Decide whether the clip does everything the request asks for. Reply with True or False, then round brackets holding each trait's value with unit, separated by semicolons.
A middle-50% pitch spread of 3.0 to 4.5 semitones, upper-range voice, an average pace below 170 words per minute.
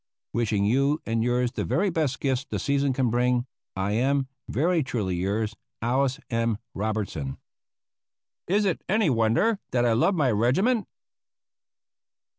False (4.1 semitones; 125 Hz; 140 wpm)